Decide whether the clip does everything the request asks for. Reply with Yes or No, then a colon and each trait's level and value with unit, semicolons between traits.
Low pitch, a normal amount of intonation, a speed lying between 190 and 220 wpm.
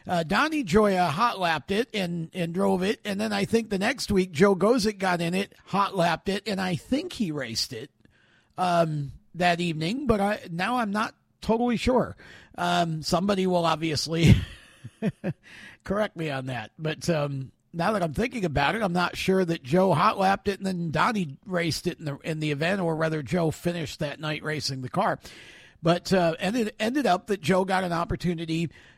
No: medium, 180 Hz; average, 3.8 semitones; average, 195 wpm